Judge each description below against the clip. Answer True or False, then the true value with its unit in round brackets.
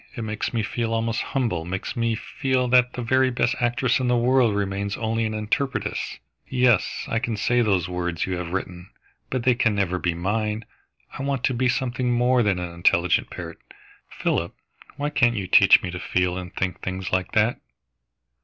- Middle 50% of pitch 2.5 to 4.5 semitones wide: False (4.9 semitones)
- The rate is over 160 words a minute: True (190 wpm)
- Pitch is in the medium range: False (115 Hz)